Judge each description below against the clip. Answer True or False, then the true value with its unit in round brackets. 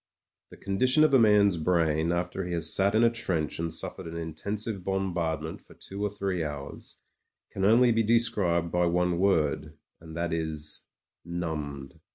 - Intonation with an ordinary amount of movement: True (3.8 semitones)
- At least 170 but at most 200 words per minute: True (175 wpm)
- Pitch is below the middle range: True (90 Hz)